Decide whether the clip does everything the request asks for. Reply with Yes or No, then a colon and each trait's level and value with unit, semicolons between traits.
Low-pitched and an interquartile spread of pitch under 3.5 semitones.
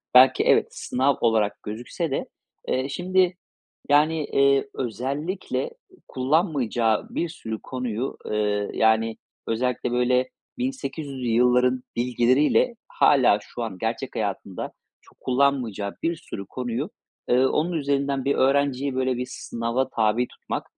Yes: low, 130 Hz; average, 3.1 semitones